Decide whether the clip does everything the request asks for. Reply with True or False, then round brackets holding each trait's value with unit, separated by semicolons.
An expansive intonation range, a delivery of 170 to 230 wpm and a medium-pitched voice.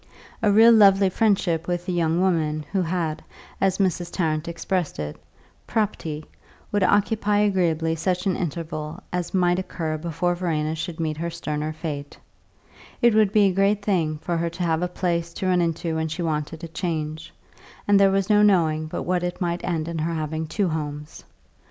False (3.1 semitones; 185 wpm; 170 Hz)